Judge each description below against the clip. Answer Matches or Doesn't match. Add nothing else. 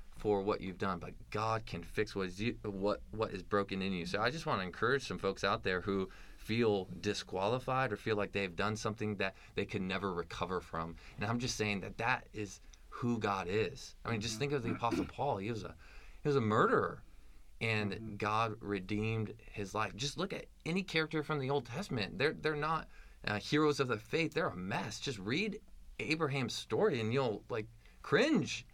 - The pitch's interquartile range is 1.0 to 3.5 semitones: Doesn't match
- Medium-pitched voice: Doesn't match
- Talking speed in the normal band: Doesn't match